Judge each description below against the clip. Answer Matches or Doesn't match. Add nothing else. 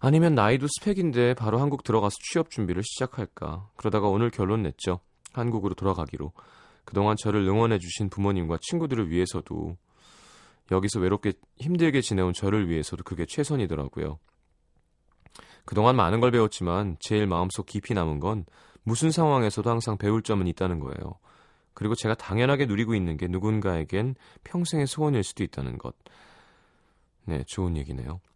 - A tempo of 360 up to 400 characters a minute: Matches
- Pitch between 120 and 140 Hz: Doesn't match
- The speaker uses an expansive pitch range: Doesn't match